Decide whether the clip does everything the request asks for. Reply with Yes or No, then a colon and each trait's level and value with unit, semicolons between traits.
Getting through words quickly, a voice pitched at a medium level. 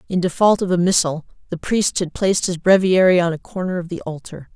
Yes: fast, 225 wpm; medium, 180 Hz